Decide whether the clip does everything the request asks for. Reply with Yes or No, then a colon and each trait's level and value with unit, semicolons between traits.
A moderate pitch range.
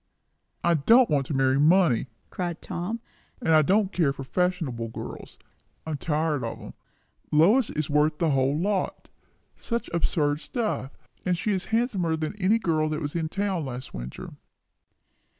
Yes: average, 4.5 semitones